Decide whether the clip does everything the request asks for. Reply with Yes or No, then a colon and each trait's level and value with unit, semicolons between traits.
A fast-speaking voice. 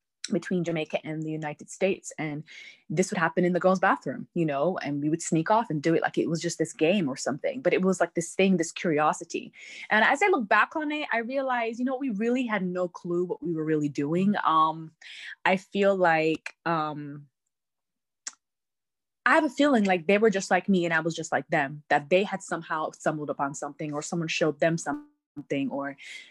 Yes: fast, 215 wpm